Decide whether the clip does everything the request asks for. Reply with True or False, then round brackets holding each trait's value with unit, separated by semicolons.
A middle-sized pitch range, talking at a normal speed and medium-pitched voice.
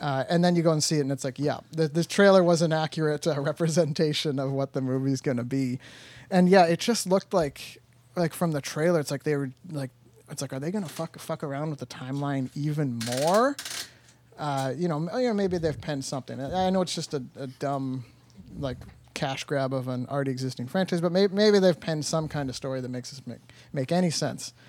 False (4.3 semitones; 235 wpm; 150 Hz)